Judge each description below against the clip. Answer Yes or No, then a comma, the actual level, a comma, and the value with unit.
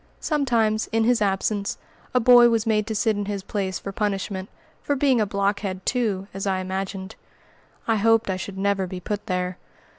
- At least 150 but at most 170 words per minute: No, average, 185 wpm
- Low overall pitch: No, high, 205 Hz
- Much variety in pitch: No, average, 2.7 semitones